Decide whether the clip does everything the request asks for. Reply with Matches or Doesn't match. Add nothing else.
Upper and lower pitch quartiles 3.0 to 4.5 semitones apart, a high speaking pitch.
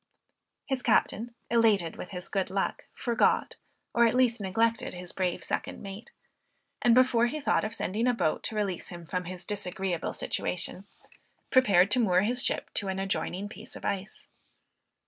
Matches